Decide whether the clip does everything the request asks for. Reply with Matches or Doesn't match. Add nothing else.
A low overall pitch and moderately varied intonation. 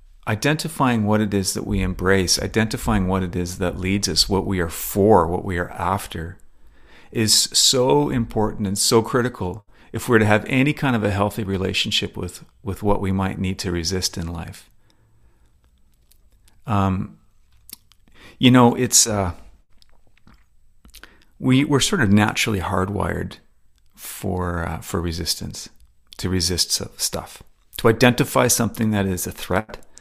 Matches